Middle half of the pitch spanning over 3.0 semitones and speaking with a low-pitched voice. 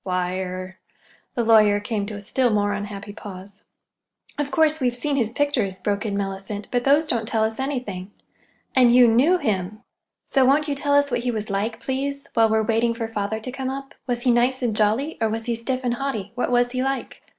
No: average, 4.2 semitones; high, 230 Hz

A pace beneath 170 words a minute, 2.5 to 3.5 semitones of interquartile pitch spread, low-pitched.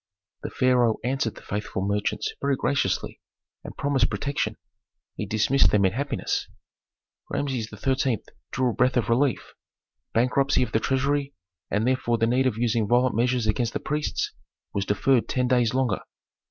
Yes: average, 155 wpm; average, 3.2 semitones; low, 125 Hz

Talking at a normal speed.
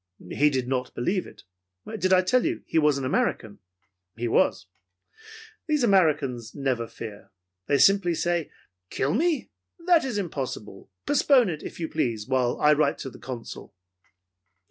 Yes: average, 155 wpm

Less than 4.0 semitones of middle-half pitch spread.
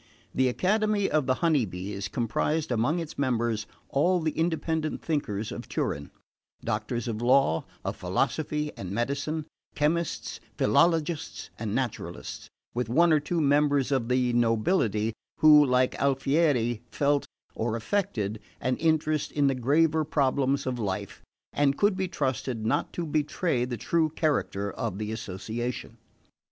No: average, 5.2 semitones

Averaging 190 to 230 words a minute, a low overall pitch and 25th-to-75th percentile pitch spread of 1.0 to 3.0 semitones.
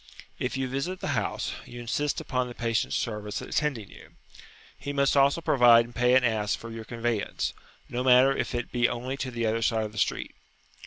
Yes: fast, 205 wpm; low, 120 Hz; narrow, 2.5 semitones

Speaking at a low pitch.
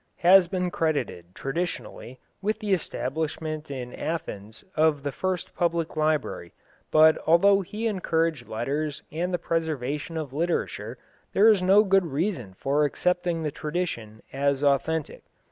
No: medium, 160 Hz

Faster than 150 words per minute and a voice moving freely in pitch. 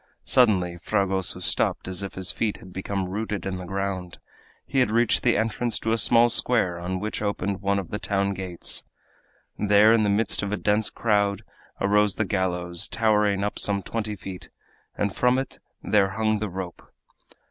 No: average, 180 wpm; narrow, 2.5 semitones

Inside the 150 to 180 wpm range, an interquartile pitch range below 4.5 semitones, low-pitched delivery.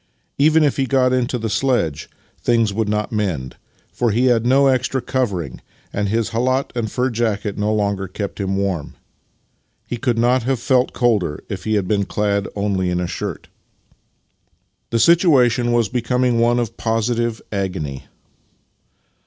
Yes: average, 160 wpm; average, 3.7 semitones; low, 115 Hz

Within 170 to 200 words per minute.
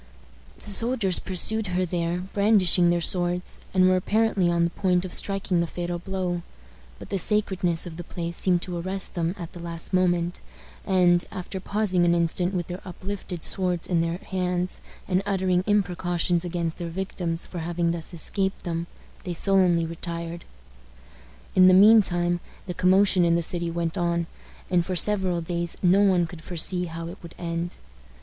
Yes: average, 175 wpm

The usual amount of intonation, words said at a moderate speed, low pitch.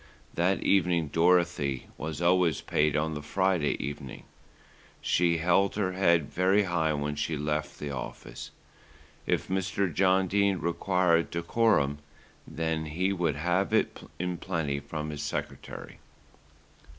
No: average, 3.5 semitones; slow, 130 wpm; very low, 85 Hz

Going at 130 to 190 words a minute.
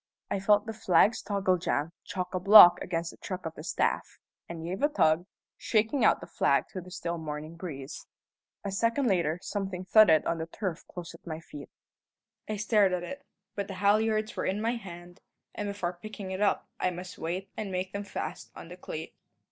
No: fast, 205 wpm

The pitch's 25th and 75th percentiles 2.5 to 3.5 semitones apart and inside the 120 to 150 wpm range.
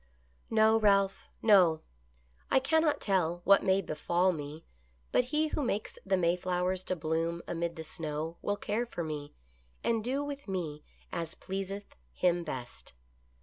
No: average, 4.3 semitones; average, 145 wpm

